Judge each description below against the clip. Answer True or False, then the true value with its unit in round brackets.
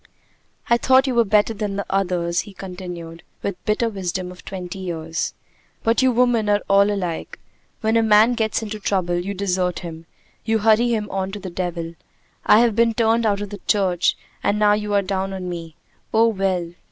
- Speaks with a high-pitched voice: True (200 Hz)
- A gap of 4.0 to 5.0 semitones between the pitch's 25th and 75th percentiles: False (3.4 semitones)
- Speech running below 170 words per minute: False (200 wpm)